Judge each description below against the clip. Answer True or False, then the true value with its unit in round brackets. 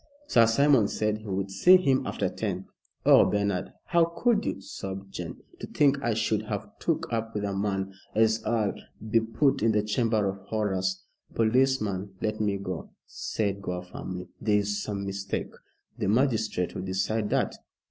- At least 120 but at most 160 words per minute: False (170 wpm)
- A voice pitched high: False (105 Hz)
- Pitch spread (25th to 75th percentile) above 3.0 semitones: False (2.7 semitones)